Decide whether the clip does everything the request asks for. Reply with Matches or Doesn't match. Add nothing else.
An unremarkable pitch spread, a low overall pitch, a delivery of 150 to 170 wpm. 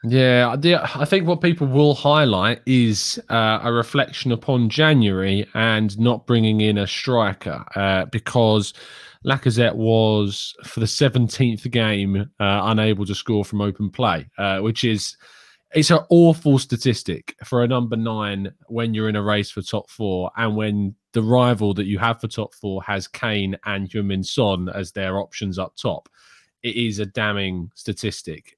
Matches